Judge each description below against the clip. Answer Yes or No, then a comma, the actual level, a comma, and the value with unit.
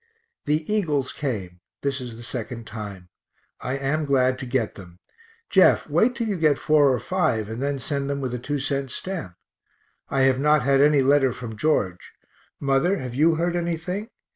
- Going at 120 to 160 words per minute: No, average, 185 wpm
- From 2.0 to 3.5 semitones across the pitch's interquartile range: No, average, 3.9 semitones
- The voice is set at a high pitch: No, low, 135 Hz